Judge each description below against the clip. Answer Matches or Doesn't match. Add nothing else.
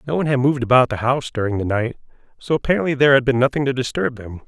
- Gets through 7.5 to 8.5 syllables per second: Matches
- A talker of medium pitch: Doesn't match